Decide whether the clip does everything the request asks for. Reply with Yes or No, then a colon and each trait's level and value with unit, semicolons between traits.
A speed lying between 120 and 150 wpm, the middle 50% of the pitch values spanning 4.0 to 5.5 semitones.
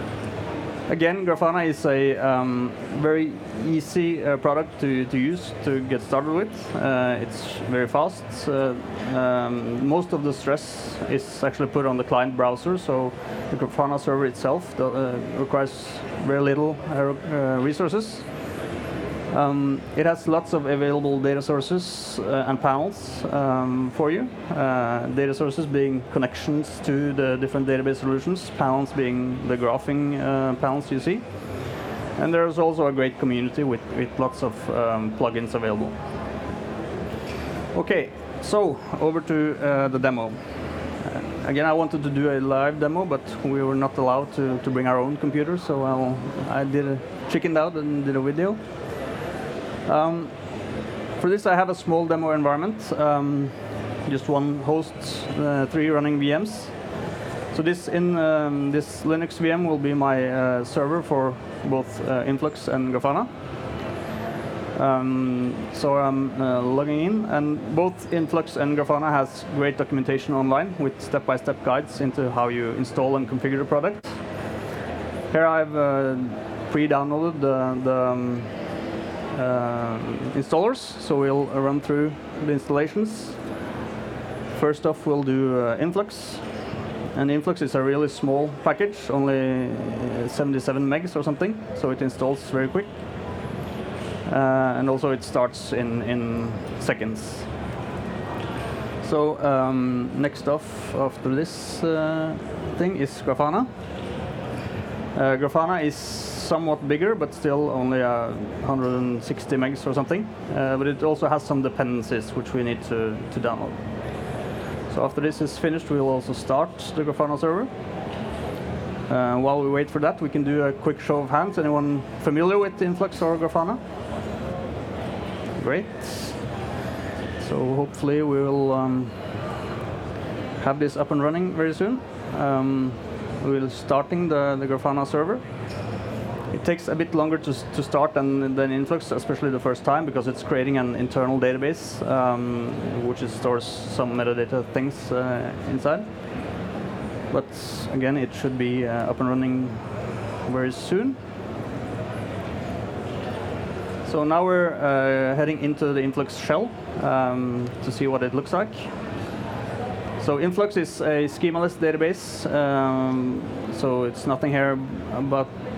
No: average, 140 wpm; average, 3.1 semitones